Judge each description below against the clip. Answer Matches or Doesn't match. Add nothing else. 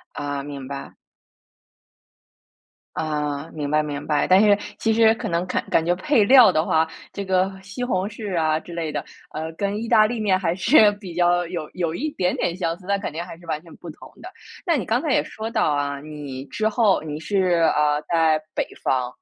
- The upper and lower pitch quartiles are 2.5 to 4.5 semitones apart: Doesn't match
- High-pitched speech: Doesn't match